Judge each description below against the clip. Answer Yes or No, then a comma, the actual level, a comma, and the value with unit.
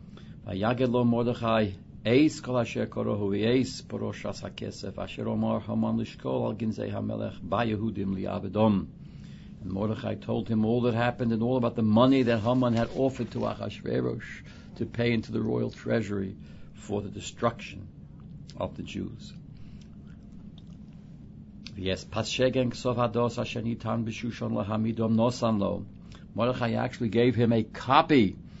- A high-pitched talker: No, low, 115 Hz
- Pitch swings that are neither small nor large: No, narrow, 2.1 semitones